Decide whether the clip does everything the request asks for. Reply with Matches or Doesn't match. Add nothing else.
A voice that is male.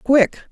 Doesn't match